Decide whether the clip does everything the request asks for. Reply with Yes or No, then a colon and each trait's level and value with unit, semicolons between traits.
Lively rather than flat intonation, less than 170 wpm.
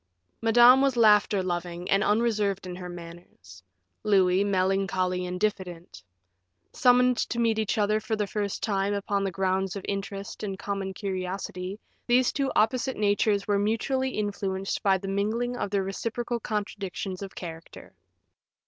No: narrow, 2.5 semitones; average, 150 wpm